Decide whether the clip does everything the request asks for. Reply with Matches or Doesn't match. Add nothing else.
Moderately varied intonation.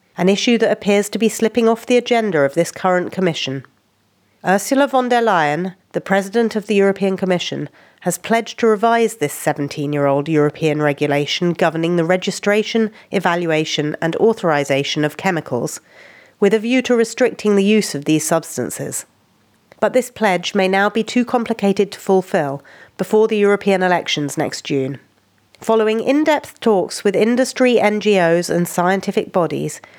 Doesn't match